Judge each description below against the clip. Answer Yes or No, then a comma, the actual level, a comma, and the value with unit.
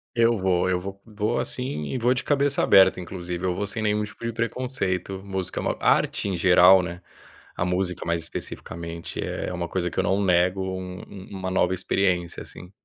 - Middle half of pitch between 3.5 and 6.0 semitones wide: No, narrow, 2.6 semitones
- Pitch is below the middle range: Yes, very low, 95 Hz